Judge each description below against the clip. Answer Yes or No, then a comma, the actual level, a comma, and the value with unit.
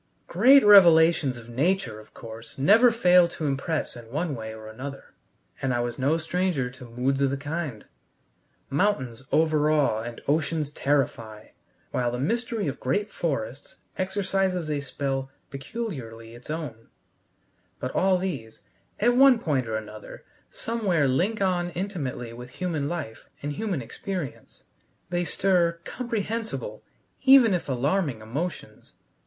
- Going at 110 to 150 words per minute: Yes, slow, 135 wpm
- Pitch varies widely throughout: Yes, wide, 6.8 semitones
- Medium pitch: Yes, medium, 150 Hz